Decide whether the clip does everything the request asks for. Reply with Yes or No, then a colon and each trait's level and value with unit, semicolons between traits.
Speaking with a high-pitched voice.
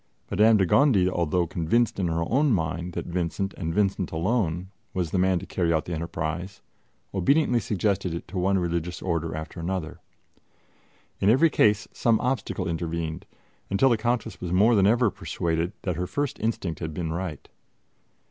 No: very low, 90 Hz